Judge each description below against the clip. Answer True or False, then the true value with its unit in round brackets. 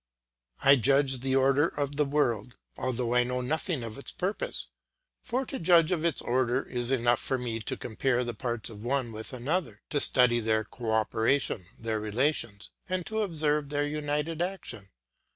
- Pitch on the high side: False (130 Hz)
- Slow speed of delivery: False (180 wpm)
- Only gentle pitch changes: False (4.0 semitones)